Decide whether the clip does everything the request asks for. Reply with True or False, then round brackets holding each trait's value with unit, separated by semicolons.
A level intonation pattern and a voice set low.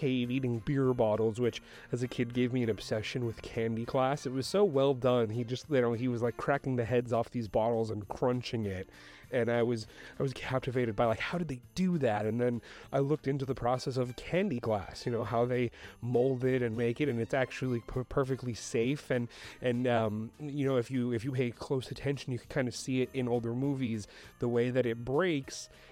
True (2.2 semitones; 125 Hz)